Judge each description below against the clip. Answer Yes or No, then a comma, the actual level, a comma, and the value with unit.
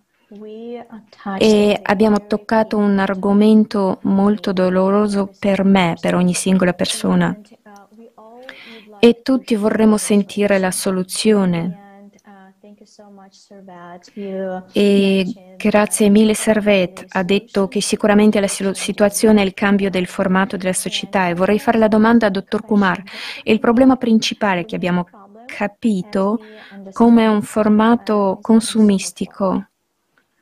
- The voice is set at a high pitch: Yes, high, 205 Hz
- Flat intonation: Yes, narrow, 2.0 semitones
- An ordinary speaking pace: No, slow, 110 wpm